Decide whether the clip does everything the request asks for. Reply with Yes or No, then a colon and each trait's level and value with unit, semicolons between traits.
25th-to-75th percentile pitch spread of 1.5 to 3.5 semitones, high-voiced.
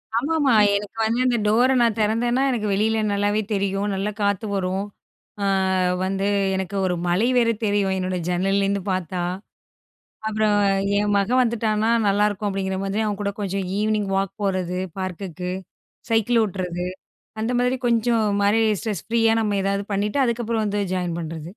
Yes: narrow, 2.6 semitones; high, 205 Hz